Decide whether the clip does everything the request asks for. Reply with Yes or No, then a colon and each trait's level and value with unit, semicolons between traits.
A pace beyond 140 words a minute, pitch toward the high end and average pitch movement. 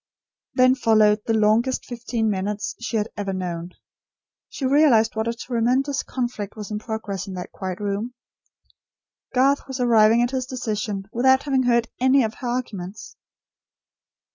Yes: average, 150 wpm; high, 230 Hz; average, 3.4 semitones